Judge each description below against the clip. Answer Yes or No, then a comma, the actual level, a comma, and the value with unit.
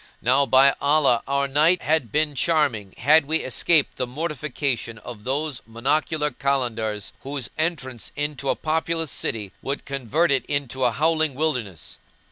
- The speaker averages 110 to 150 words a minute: Yes, average, 145 wpm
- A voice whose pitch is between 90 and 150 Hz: Yes, medium, 140 Hz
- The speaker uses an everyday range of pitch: Yes, average, 3.9 semitones